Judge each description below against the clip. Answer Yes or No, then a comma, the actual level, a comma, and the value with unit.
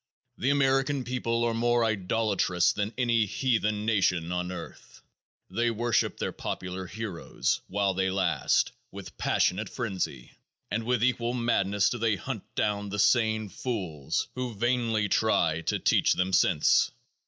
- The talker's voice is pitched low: Yes, low, 110 Hz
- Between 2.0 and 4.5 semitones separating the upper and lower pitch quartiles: Yes, average, 3.9 semitones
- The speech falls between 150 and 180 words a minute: No, average, 140 wpm